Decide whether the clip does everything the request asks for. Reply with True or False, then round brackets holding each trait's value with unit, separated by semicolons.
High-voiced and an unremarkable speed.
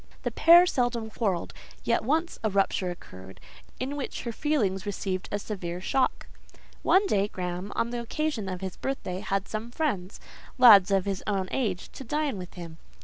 True (205 Hz; 165 wpm)